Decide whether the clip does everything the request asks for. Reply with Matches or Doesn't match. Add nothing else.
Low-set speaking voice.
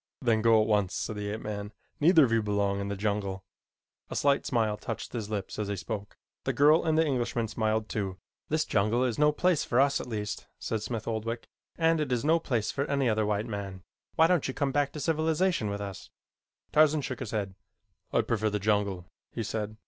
Matches